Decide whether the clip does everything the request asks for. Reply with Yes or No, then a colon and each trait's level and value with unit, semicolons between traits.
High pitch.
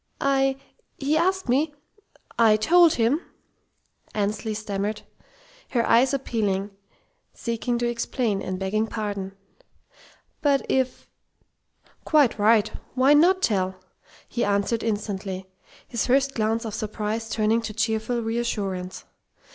Yes: high, 225 Hz